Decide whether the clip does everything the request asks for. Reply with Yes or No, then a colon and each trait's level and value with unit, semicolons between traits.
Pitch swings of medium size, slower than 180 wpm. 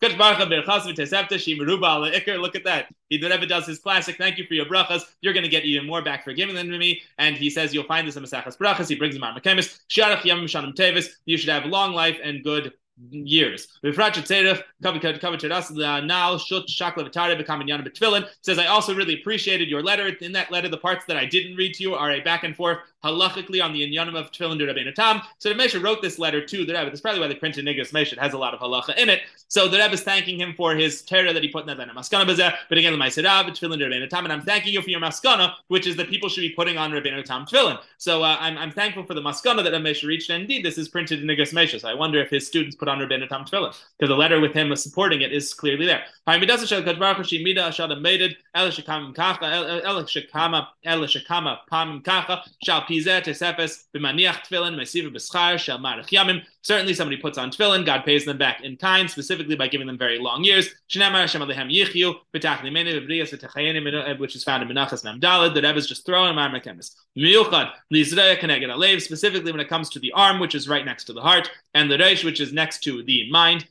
No: average, 3.8 semitones; average, 185 wpm